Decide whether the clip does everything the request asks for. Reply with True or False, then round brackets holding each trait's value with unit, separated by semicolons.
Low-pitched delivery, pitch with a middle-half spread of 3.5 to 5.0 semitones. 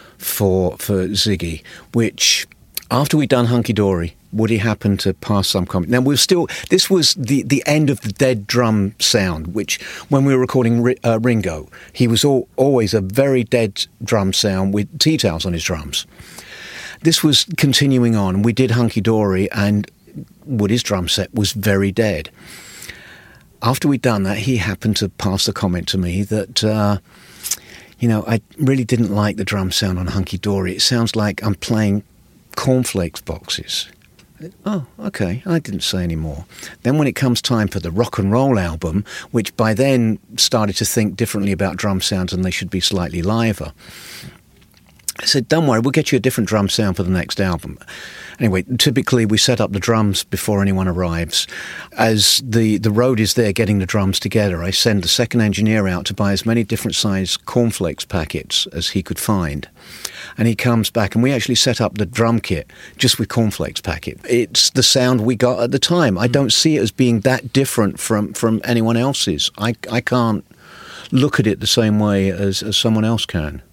True (110 Hz; 4.1 semitones)